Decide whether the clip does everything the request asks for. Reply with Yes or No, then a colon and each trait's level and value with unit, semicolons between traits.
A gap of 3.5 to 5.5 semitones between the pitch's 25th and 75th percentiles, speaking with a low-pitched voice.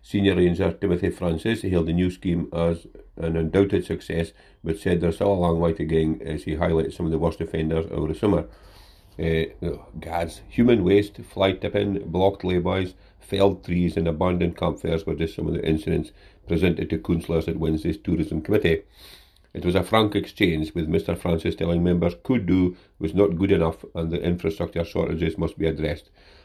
No: average, 3.1 semitones; very low, 85 Hz